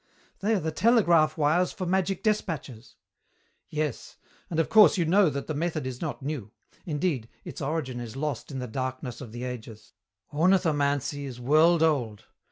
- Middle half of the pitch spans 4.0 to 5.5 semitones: Yes, average, 5.0 semitones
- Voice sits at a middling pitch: Yes, medium, 150 Hz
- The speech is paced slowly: No, average, 170 wpm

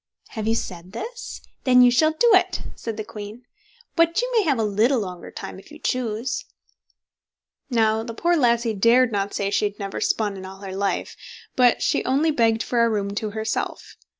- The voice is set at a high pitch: Yes, high, 225 Hz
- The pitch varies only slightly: No, average, 3.7 semitones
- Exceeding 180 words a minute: Yes, average, 200 wpm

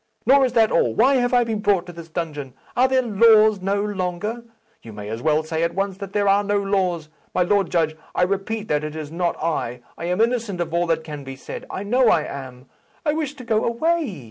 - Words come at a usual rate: No, fast, 240 wpm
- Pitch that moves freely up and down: Yes, wide, 5.7 semitones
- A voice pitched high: Yes, high, 195 Hz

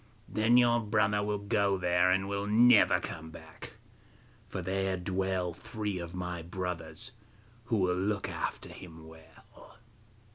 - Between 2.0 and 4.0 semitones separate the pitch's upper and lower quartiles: Yes, average, 2.8 semitones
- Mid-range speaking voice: No, very low, 95 Hz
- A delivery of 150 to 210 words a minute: No, average, 140 wpm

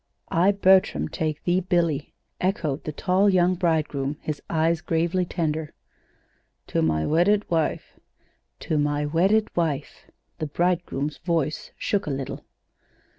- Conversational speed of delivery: No, slow, 125 wpm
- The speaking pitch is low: No, medium, 165 Hz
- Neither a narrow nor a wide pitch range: Yes, average, 3.4 semitones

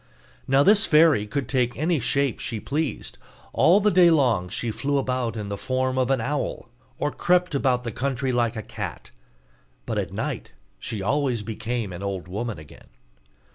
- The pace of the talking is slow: No, average, 175 wpm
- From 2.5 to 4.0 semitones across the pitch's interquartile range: No, average, 4.4 semitones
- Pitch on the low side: Yes, low, 130 Hz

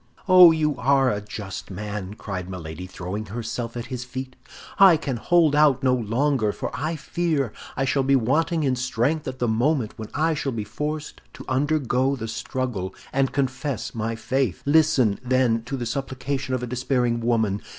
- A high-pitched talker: No, low, 130 Hz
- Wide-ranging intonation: No, average, 3.9 semitones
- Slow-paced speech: No, average, 180 wpm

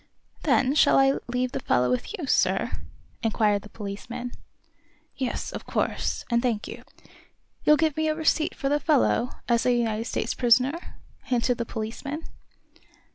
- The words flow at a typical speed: Yes, average, 155 wpm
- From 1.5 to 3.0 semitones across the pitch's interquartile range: No, average, 3.8 semitones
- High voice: Yes, very high, 250 Hz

